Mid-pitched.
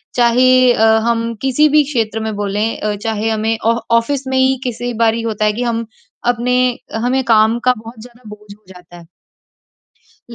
No: high, 230 Hz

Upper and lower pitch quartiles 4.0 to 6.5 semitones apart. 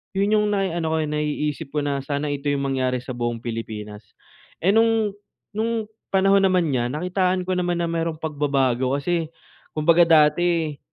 Yes: average, 4.7 semitones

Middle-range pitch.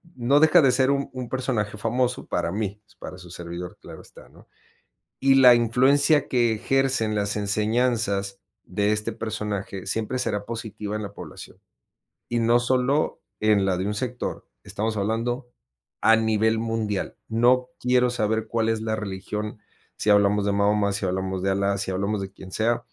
No: low, 110 Hz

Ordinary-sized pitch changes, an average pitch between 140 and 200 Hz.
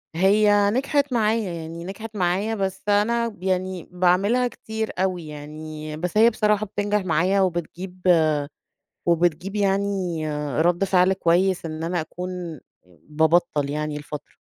Yes: average, 3.6 semitones; medium, 185 Hz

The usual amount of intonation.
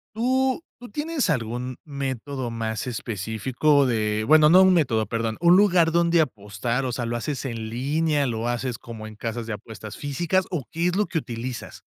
No: wide, 6.3 semitones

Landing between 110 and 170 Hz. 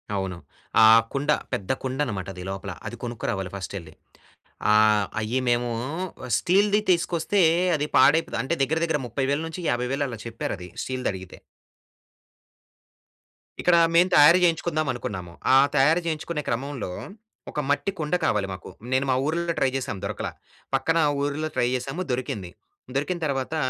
Yes: low, 135 Hz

